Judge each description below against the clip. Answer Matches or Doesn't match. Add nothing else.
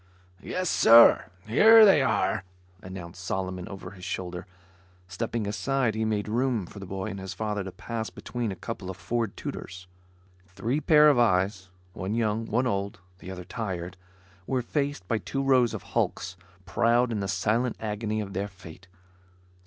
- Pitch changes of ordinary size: Matches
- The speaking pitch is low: Matches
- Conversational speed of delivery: Matches